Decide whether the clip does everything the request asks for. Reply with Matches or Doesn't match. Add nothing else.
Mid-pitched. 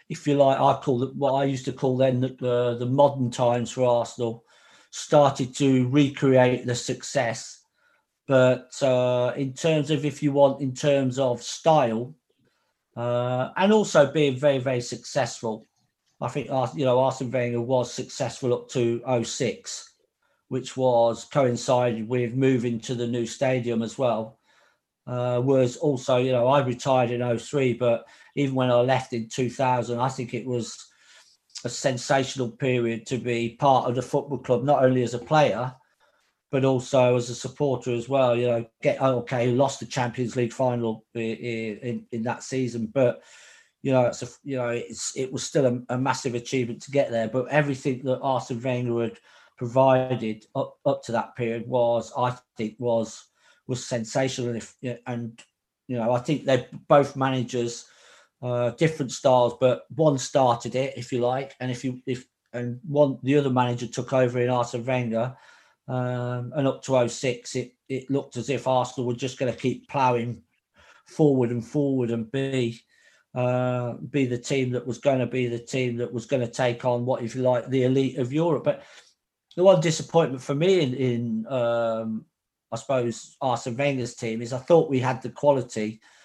Doesn't match